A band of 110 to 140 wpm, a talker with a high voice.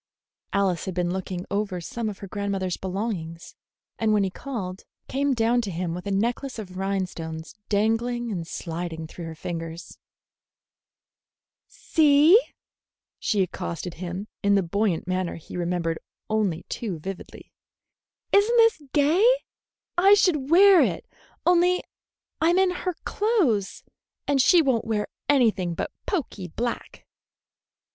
Yes: slow, 135 wpm; high, 200 Hz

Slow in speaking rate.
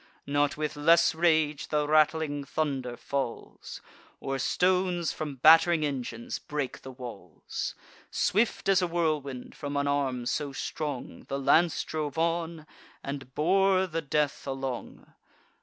Yes: slow, 130 wpm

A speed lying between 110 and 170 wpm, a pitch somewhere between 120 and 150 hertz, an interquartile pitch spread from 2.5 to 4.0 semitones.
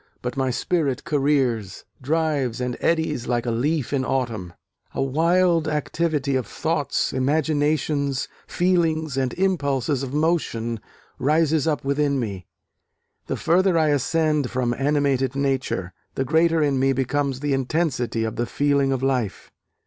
Yes: average, 140 wpm; medium, 140 Hz; average, 3.5 semitones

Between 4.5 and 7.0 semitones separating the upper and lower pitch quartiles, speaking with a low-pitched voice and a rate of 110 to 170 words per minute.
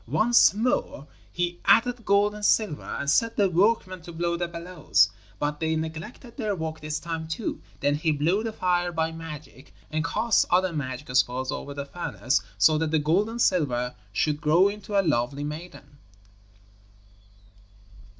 No: average, 4.8 semitones; medium, 165 Hz; average, 165 wpm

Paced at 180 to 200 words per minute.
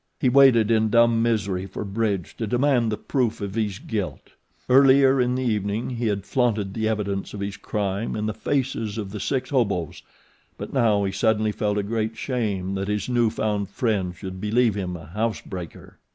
Yes: average, 195 wpm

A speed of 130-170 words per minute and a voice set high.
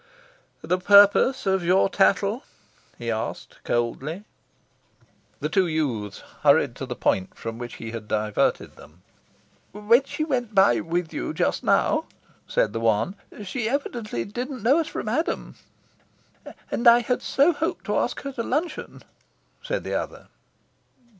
Yes: average, 145 wpm; high, 195 Hz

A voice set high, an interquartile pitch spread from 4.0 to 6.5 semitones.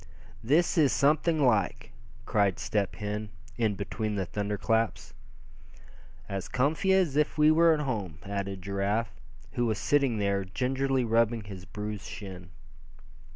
No: low, 110 Hz; wide, 5.5 semitones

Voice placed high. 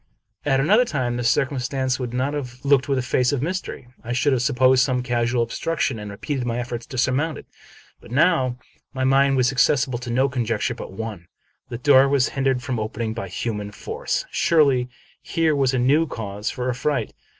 No: low, 130 Hz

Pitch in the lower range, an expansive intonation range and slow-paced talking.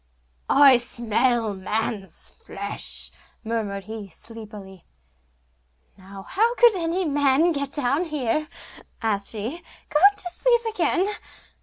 No: high, 245 Hz; wide, 7.2 semitones; slow, 110 wpm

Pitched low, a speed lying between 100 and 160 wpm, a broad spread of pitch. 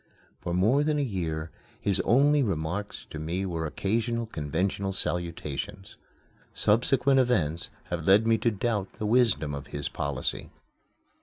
Yes: very low, 95 Hz; average, 140 wpm; wide, 6.1 semitones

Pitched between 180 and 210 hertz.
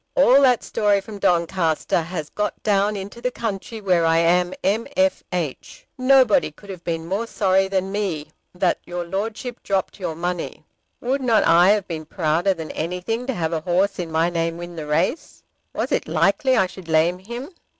Yes: high, 190 Hz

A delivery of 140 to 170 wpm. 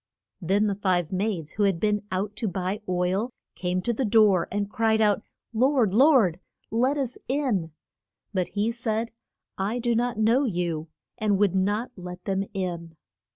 Yes: average, 165 wpm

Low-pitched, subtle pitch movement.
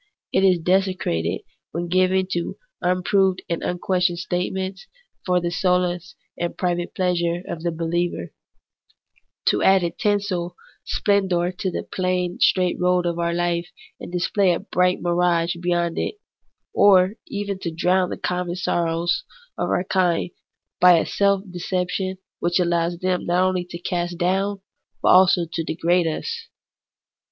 No: medium, 180 Hz; narrow, 1.3 semitones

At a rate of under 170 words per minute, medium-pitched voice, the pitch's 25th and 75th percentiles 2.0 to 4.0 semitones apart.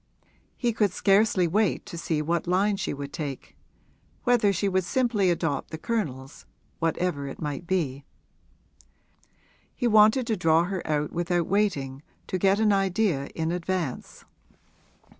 No: average, 140 wpm; medium, 180 Hz; average, 4.5 semitones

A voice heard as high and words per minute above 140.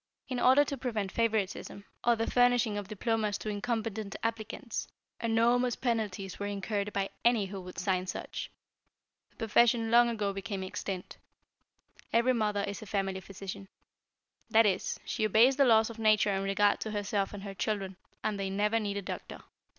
Yes: high, 210 Hz; average, 170 wpm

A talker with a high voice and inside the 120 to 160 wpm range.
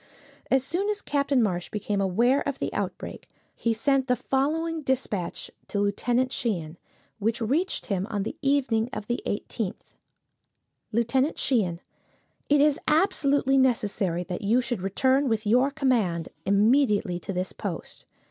Yes: high, 240 Hz; average, 145 wpm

